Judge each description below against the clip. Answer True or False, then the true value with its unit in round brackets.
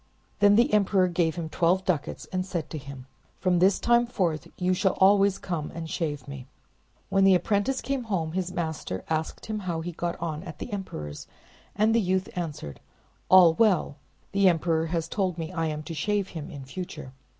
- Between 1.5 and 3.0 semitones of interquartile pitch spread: False (3.5 semitones)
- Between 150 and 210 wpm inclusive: True (200 wpm)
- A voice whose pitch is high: False (175 Hz)